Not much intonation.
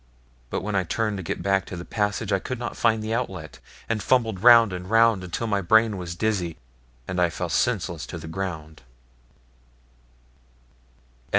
No: average, 3.8 semitones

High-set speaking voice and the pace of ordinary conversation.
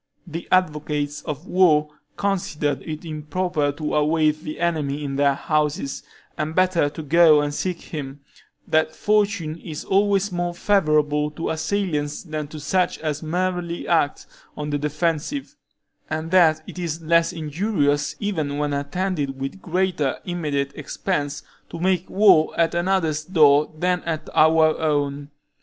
No: medium, 155 Hz; average, 145 wpm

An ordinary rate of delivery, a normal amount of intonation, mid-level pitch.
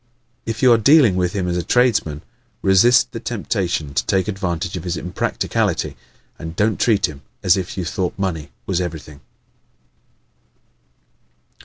No: average, 150 wpm; average, 3.7 semitones; very low, 95 Hz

